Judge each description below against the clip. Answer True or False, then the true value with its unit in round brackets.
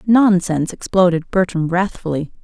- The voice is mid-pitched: True (180 Hz)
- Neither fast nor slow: False (100 wpm)